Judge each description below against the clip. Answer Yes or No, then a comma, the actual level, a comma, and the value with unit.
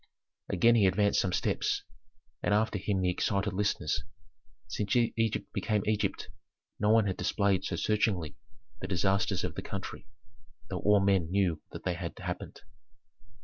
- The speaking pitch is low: Yes, low, 100 Hz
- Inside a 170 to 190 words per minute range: No, average, 150 wpm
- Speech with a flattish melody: Yes, narrow, 2.2 semitones